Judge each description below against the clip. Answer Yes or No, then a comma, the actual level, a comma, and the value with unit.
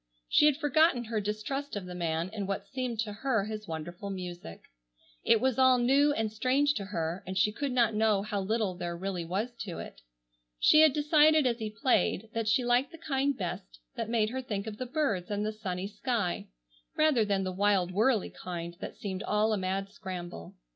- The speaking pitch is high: Yes, high, 215 Hz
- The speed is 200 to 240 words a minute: Yes, fast, 205 wpm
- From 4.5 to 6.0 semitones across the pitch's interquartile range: Yes, average, 5.2 semitones